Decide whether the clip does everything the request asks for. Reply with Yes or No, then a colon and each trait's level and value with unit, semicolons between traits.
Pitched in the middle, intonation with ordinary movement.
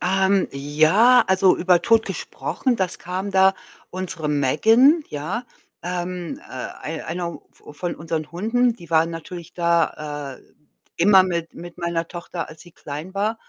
Yes: medium, 175 Hz; average, 3.1 semitones